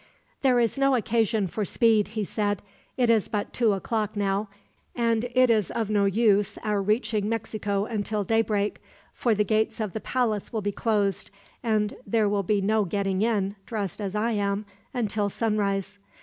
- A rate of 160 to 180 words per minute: Yes, average, 175 wpm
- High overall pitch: Yes, high, 210 Hz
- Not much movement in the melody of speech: Yes, narrow, 1.9 semitones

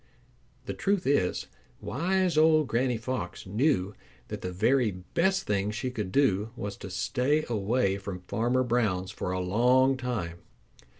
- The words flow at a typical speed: Yes, average, 145 wpm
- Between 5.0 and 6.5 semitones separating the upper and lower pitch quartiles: Yes, wide, 5.5 semitones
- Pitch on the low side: Yes, low, 115 Hz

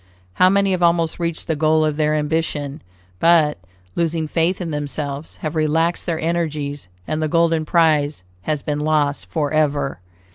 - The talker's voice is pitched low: No, medium, 155 Hz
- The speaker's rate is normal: Yes, average, 155 wpm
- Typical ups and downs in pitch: No, narrow, 1.9 semitones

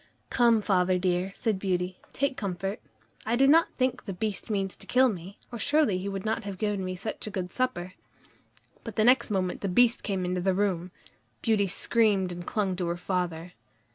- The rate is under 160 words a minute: No, average, 200 wpm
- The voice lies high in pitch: Yes, high, 195 Hz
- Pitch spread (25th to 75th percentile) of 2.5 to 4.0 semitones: Yes, average, 3.5 semitones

